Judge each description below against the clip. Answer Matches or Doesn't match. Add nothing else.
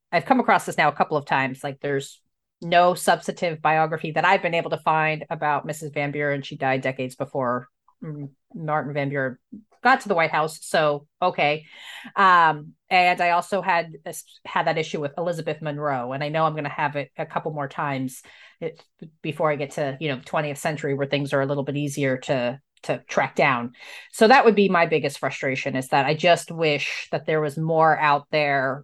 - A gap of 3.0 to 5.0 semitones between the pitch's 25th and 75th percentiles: Doesn't match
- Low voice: Doesn't match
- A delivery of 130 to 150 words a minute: Doesn't match